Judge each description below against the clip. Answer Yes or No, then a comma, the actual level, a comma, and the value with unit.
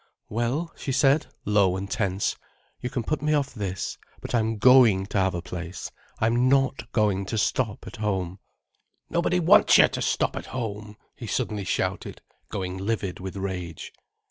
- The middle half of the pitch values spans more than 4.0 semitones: Yes, average, 4.9 semitones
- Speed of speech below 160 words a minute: No, average, 170 wpm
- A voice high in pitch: No, low, 105 Hz